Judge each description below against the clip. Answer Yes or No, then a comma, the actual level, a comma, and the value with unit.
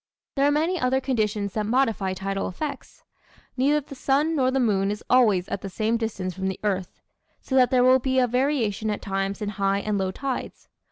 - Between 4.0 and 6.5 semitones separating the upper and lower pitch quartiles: Yes, average, 5.1 semitones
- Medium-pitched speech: No, high, 225 Hz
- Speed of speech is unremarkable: No, fast, 210 wpm